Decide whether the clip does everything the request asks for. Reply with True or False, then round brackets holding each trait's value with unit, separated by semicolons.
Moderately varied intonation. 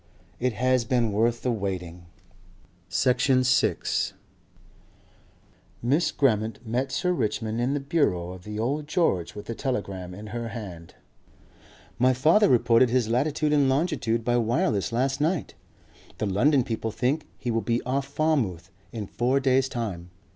True (3.9 semitones)